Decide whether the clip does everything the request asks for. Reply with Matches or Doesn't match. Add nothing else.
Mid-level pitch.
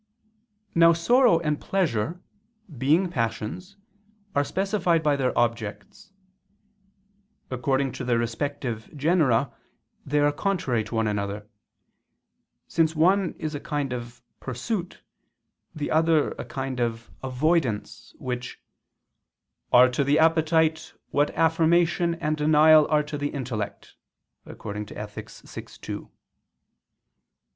Matches